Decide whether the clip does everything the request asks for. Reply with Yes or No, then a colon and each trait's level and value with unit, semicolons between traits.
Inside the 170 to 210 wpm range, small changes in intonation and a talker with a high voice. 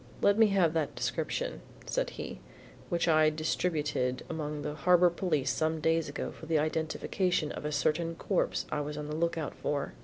No: average, 180 wpm; narrow, 2.1 semitones; medium, 155 Hz